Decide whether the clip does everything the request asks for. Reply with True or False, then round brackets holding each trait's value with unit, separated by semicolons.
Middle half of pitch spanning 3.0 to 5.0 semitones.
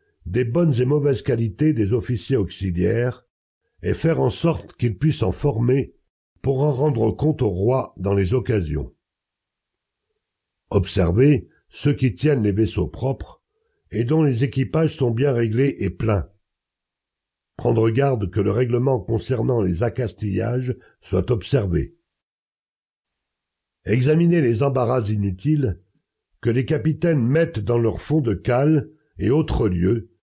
False (5.6 semitones)